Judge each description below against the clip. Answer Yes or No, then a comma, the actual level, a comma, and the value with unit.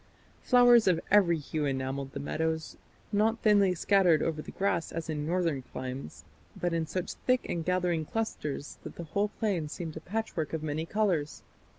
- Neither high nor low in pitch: Yes, medium, 165 Hz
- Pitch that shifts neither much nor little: Yes, average, 4.6 semitones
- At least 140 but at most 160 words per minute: No, average, 175 wpm